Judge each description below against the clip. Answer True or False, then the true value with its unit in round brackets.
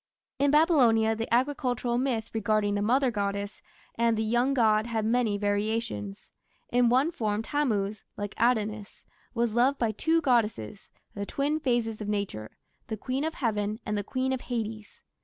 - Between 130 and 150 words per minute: False (160 wpm)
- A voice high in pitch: True (225 Hz)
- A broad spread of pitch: False (3.1 semitones)